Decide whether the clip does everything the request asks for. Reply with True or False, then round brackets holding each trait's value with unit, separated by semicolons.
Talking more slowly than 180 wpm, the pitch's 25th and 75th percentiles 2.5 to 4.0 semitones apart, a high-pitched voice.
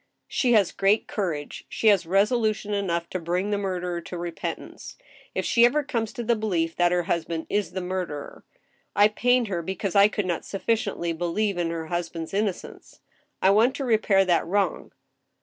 False (185 wpm; 3.6 semitones; 195 Hz)